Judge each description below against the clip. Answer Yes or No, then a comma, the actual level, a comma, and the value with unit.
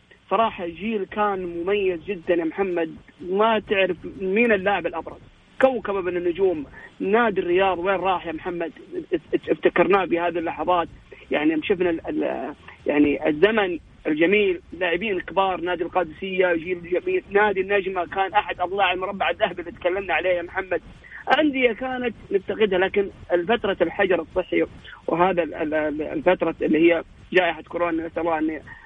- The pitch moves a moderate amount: Yes, average, 3.1 semitones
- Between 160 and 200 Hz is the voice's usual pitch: Yes, medium, 185 Hz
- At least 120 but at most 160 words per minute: Yes, average, 130 wpm